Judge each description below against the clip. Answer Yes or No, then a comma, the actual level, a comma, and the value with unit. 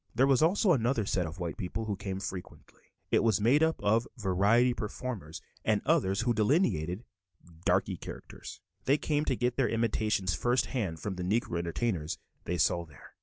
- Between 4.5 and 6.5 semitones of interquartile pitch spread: Yes, average, 5.1 semitones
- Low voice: Yes, low, 105 Hz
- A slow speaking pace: No, average, 175 wpm